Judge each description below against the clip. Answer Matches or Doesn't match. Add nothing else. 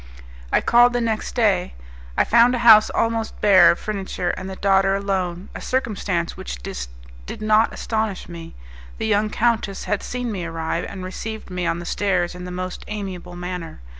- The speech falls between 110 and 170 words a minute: Doesn't match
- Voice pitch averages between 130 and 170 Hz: Doesn't match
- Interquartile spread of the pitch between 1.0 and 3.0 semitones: Doesn't match